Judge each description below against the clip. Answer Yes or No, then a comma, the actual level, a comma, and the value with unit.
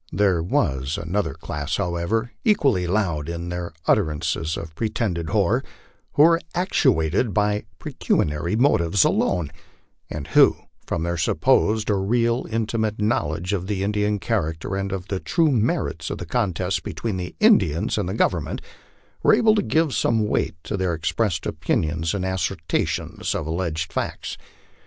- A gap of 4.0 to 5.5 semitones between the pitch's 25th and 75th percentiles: Yes, average, 4.9 semitones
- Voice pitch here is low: Yes, very low, 95 Hz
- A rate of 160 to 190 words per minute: No, average, 150 wpm